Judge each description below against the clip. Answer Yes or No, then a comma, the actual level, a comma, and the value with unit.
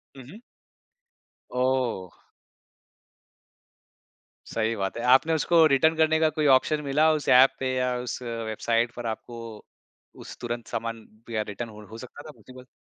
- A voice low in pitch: Yes, low, 125 Hz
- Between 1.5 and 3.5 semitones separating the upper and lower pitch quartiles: No, average, 4.0 semitones